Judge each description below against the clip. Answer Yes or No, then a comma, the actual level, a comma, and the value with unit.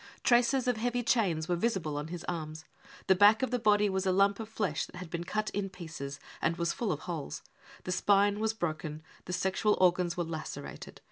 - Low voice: No, medium, 185 Hz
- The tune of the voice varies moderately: Yes, average, 4.3 semitones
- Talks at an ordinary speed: No, fast, 210 wpm